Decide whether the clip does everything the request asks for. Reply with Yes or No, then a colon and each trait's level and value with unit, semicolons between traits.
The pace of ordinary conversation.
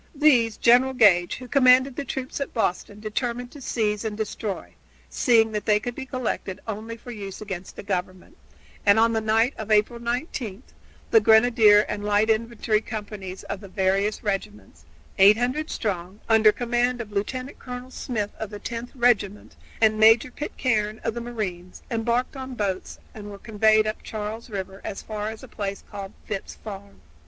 Yes: average, 170 wpm